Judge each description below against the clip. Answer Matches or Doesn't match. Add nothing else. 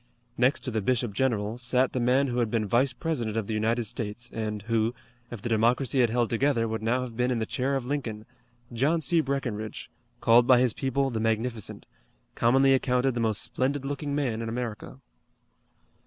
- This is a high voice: Doesn't match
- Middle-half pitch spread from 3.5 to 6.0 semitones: Doesn't match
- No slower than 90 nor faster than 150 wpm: Doesn't match